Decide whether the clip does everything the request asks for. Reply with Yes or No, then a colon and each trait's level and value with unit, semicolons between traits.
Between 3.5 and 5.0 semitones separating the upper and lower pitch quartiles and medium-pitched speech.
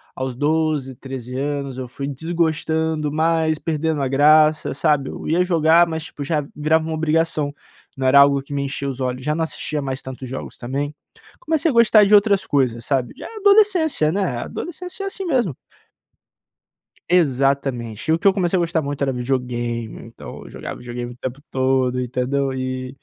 Yes: average, 3.8 semitones; medium, 145 Hz